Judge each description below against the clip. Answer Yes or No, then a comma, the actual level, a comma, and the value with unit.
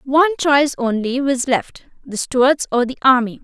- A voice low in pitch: No, very high, 260 Hz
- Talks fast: No, average, 175 wpm